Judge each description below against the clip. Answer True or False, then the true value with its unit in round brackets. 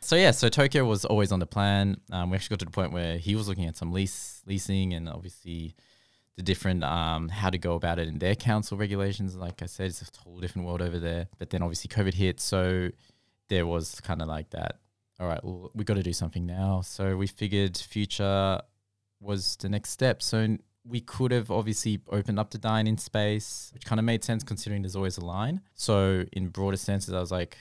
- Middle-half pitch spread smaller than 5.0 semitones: True (2.9 semitones)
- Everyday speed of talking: False (230 wpm)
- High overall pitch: False (100 Hz)